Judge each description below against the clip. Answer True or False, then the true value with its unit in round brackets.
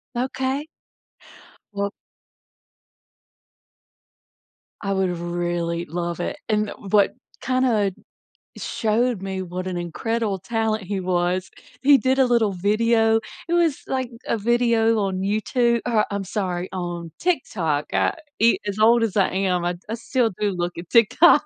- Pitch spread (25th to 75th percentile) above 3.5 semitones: True (4.4 semitones)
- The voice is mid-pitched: False (205 Hz)